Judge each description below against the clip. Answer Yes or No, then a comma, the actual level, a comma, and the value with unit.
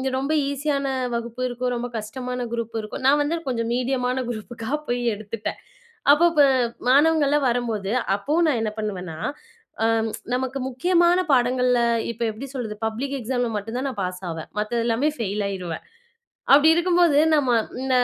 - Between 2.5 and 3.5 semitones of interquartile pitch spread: No, average, 3.9 semitones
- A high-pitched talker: Yes, very high, 250 Hz